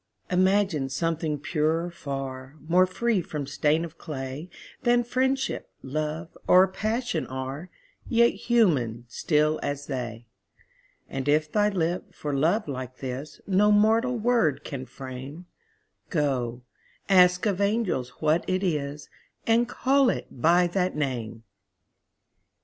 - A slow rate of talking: Yes, slow, 125 wpm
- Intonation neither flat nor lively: No, wide, 6.5 semitones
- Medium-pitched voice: Yes, medium, 160 Hz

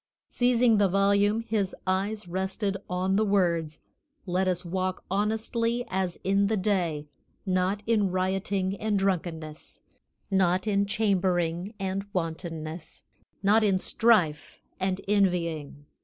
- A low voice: No, high, 190 Hz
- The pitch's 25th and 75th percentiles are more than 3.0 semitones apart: No, narrow, 2.4 semitones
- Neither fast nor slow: No, slow, 120 wpm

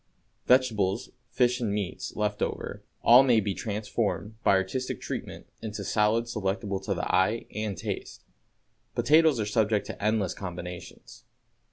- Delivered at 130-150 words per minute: Yes, average, 140 wpm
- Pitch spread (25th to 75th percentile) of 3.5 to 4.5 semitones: No, average, 2.9 semitones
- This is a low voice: Yes, low, 105 Hz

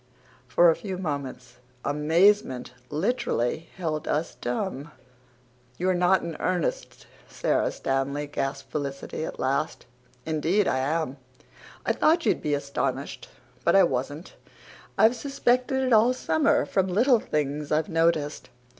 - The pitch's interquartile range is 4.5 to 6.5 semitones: Yes, average, 5.2 semitones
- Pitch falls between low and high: Yes, medium, 160 Hz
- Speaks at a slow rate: Yes, slow, 130 wpm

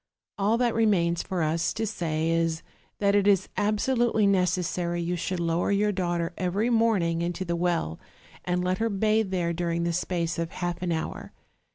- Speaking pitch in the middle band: Yes, medium, 180 Hz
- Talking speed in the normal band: Yes, average, 185 wpm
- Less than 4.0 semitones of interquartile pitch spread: Yes, average, 3.3 semitones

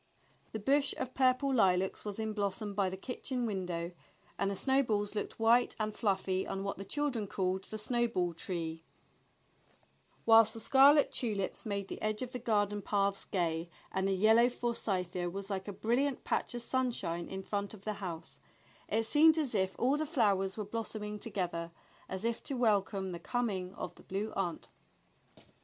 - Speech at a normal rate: Yes, average, 175 wpm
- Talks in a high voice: Yes, high, 205 Hz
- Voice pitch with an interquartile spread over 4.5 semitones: No, average, 3.8 semitones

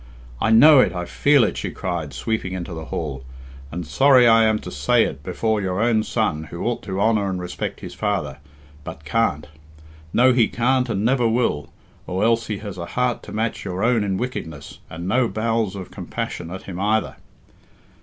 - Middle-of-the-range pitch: No, low, 105 Hz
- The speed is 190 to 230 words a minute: Yes, average, 195 wpm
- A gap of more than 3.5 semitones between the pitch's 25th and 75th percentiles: Yes, average, 4.7 semitones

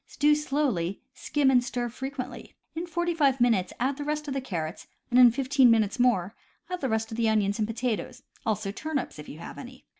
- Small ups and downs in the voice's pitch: No, average, 4.3 semitones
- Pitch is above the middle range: Yes, very high, 250 Hz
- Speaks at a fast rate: Yes, fast, 210 wpm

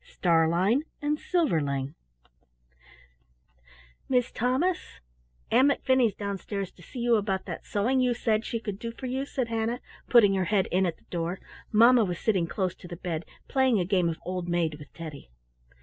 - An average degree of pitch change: No, wide, 5.9 semitones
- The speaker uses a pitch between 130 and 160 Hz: No, high, 205 Hz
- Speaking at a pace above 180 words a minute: No, average, 170 wpm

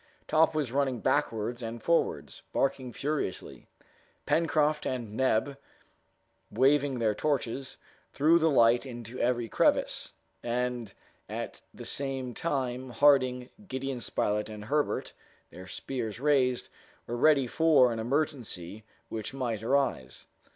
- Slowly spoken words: Yes, slow, 120 wpm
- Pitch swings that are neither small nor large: Yes, average, 3.3 semitones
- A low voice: Yes, low, 130 Hz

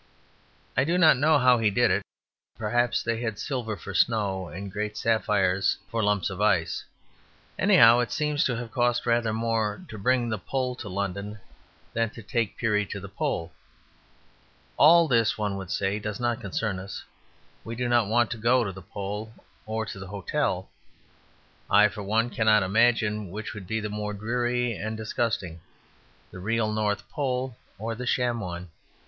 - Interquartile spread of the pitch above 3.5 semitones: No, average, 3.0 semitones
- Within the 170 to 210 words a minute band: Yes, average, 175 wpm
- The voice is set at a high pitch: No, low, 110 Hz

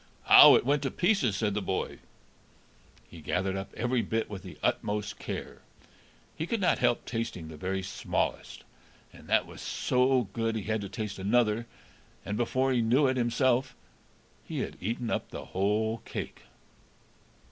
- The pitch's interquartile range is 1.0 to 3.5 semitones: No, average, 4.2 semitones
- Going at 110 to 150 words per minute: No, average, 165 wpm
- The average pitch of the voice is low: Yes, low, 115 Hz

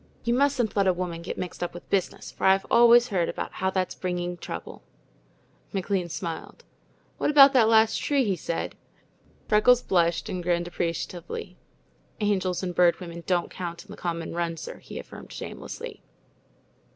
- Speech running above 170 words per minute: No, average, 165 wpm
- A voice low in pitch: No, medium, 180 Hz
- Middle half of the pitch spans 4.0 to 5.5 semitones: No, average, 3.6 semitones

